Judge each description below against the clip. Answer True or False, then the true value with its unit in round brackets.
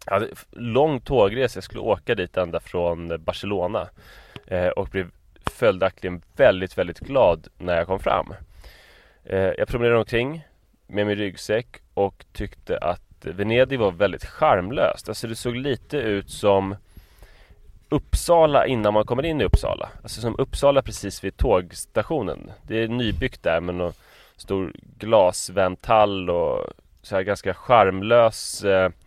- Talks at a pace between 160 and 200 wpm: False (140 wpm)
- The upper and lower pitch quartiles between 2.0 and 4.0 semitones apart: False (4.4 semitones)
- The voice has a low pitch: True (100 Hz)